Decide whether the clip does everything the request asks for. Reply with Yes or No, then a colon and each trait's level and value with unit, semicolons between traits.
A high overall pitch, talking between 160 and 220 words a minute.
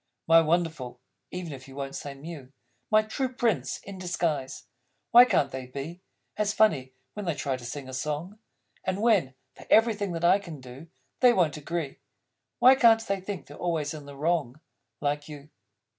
No: medium, 165 Hz; average, 180 wpm